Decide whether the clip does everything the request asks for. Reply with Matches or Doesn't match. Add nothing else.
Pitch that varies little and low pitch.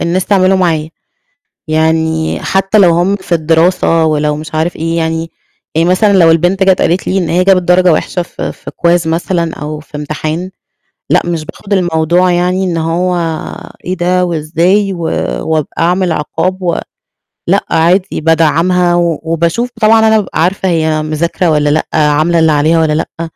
Doesn't match